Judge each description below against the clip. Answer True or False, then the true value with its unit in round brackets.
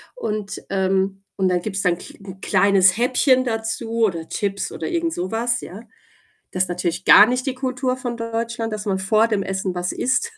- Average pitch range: True (4.0 semitones)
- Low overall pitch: False (210 Hz)